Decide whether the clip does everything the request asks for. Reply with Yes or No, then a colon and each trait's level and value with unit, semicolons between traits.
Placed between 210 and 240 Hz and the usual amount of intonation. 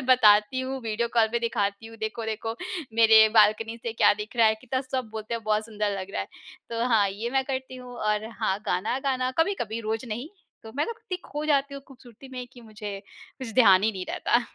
Yes: high, 225 Hz; average, 3.2 semitones